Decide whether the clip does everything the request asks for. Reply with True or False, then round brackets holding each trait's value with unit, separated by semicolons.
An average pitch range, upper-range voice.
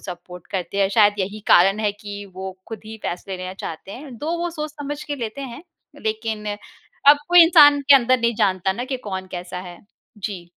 False (6.7 semitones; 215 Hz)